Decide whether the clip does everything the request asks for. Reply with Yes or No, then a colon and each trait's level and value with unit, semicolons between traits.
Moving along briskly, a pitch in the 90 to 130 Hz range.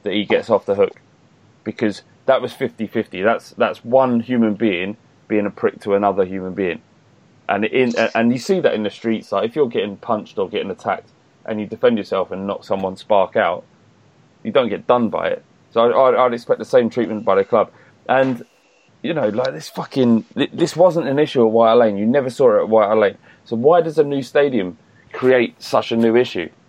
Yes: fast, 215 wpm; low, 120 Hz